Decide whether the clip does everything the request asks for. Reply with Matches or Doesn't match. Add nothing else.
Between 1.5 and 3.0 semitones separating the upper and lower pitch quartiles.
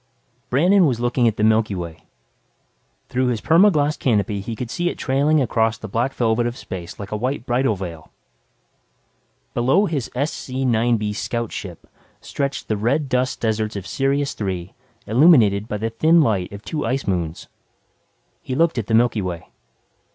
Doesn't match